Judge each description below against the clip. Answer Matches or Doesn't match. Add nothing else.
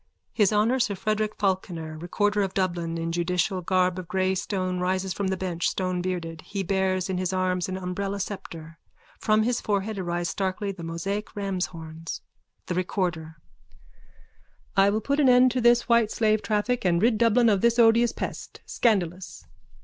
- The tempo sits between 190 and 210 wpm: Doesn't match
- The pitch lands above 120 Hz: Matches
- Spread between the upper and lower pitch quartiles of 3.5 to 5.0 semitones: Doesn't match